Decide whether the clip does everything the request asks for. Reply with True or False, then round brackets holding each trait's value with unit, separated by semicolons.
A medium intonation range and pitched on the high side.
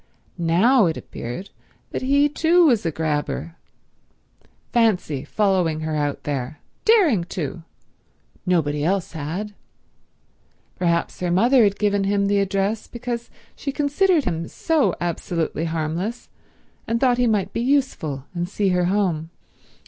False (6.5 semitones; 195 Hz)